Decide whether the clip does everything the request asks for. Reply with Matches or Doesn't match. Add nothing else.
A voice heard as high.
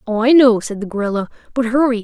Matches